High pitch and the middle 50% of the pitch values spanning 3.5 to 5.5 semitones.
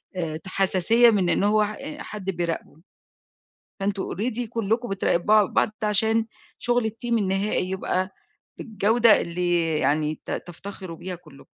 Yes: high, 195 Hz; average, 3.9 semitones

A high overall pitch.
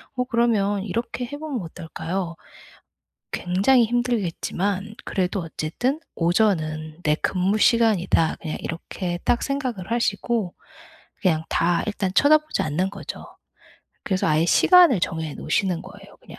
Yes: high, 195 Hz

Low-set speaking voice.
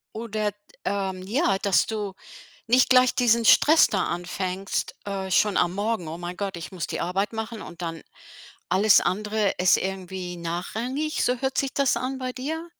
No: high, 205 Hz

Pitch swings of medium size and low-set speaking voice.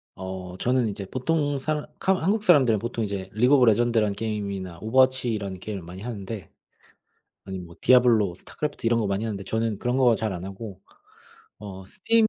Yes: average, 4.5 semitones; low, 110 Hz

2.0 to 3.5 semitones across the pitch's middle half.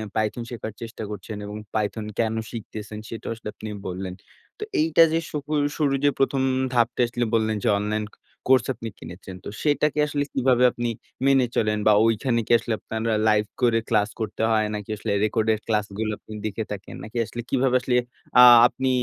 Yes: narrow, 2.6 semitones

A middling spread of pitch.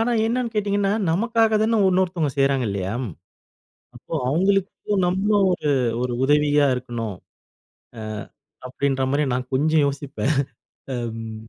No: wide, 7.2 semitones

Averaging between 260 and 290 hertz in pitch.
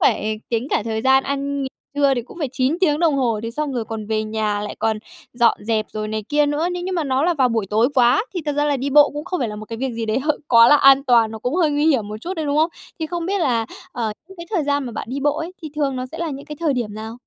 Yes: very high, 270 Hz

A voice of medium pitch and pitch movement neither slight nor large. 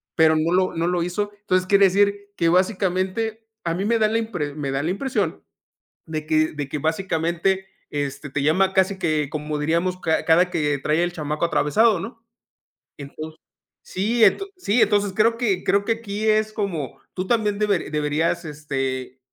Yes: medium, 180 Hz; average, 4.7 semitones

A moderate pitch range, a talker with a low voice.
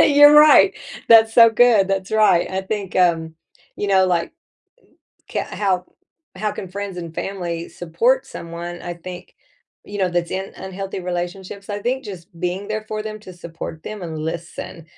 No: average, 3.4 semitones; high, 190 Hz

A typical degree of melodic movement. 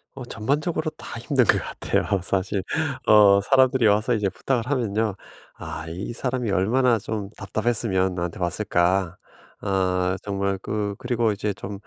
Yes: average, 3.7 semitones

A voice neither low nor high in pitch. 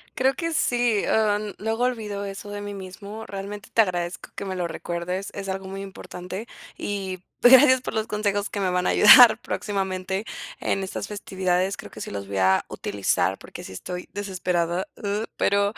No: high, 200 Hz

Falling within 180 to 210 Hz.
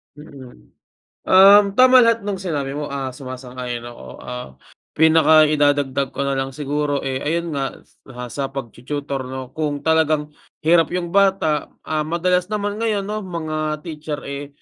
No: medium, 150 Hz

